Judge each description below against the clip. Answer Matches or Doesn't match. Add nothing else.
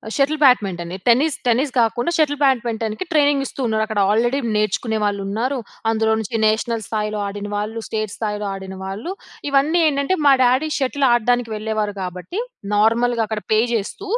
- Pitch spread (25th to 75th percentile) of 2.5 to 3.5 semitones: Doesn't match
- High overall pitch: Matches